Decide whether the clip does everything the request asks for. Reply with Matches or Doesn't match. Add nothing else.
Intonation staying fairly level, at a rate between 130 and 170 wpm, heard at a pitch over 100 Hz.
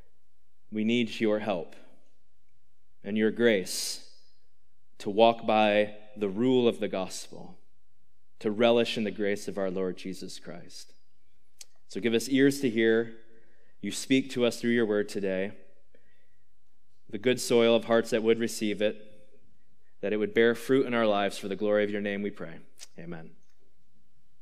Matches